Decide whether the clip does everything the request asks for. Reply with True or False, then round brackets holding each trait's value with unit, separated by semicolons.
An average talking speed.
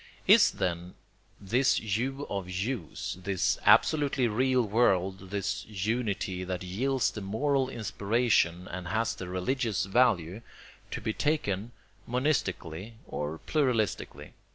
False (115 wpm)